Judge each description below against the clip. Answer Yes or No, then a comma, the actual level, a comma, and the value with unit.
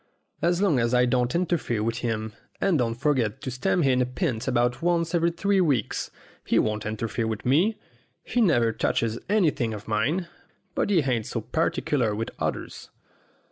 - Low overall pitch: Yes, low, 125 Hz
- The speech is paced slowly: No, average, 175 wpm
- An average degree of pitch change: No, wide, 6.8 semitones